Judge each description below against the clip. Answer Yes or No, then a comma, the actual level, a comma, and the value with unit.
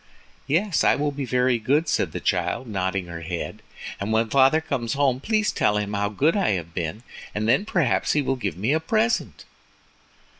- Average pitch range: No, wide, 6.6 semitones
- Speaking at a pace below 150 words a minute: No, average, 195 wpm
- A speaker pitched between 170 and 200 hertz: No, low, 125 Hz